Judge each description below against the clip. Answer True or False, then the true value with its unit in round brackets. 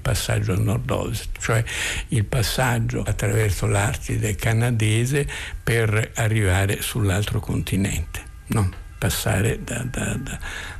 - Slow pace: True (100 wpm)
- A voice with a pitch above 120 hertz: False (110 Hz)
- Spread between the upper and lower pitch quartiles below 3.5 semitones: True (2.5 semitones)